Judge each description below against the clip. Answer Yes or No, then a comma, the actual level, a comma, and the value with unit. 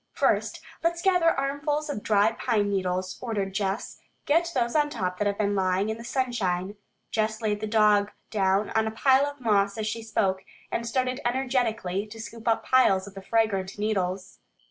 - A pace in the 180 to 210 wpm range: Yes, average, 185 wpm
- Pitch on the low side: No, high, 220 Hz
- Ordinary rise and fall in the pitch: Yes, average, 4.0 semitones